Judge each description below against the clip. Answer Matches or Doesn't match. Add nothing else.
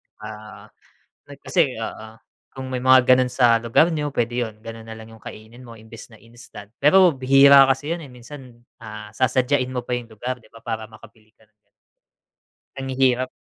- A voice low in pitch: Matches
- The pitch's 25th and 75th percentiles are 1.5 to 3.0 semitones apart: Matches